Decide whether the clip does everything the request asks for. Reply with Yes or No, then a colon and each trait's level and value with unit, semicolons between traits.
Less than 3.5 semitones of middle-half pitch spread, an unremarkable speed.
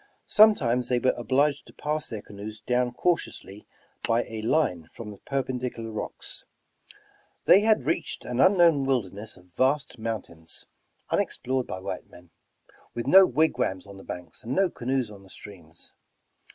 No: average, 5.3 semitones; average, 155 wpm